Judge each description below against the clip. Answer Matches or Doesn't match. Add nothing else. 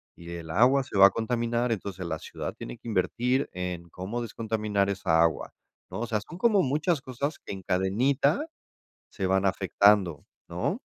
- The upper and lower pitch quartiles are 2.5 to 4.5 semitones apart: Doesn't match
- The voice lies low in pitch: Matches